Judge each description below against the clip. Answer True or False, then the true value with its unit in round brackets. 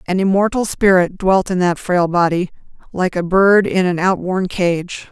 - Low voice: False (185 Hz)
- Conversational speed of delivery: True (175 wpm)